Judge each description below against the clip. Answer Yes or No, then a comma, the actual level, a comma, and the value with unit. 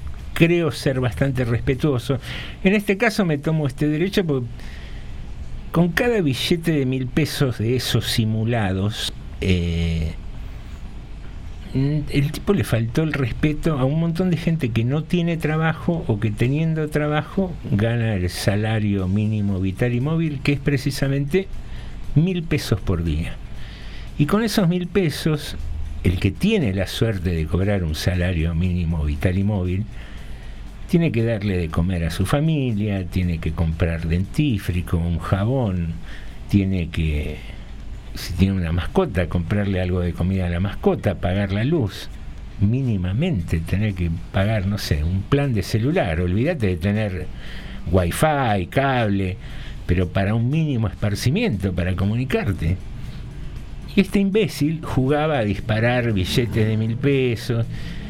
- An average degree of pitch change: No, wide, 7.7 semitones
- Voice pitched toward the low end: Yes, low, 110 Hz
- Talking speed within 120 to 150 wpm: Yes, average, 140 wpm